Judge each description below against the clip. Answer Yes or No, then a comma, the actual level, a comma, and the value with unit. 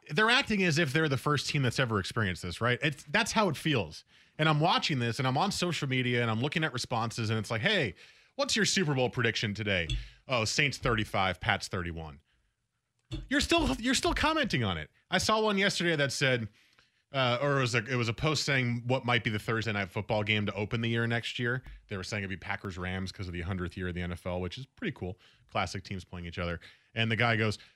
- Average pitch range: No, wide, 6.5 semitones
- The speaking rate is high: Yes, fast, 240 wpm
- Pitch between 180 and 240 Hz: No, low, 120 Hz